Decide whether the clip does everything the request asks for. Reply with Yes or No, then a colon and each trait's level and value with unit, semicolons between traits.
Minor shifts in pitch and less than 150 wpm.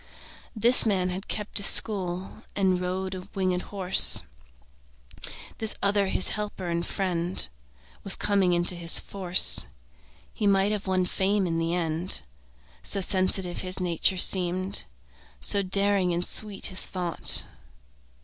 Yes: narrow, 1.8 semitones; slow, 135 wpm